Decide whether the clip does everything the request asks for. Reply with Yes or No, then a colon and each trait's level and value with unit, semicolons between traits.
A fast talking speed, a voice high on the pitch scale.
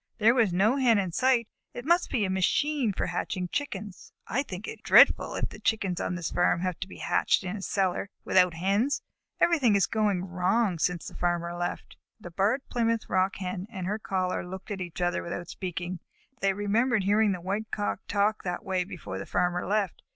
Yes: fast, 210 wpm; high, 195 Hz